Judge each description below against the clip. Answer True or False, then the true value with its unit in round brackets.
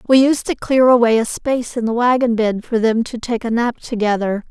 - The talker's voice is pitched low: False (235 Hz)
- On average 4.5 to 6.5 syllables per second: True (5.4 syllables/s)